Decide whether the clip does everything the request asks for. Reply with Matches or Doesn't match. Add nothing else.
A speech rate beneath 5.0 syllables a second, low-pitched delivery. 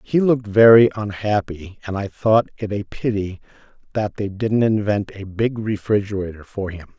Matches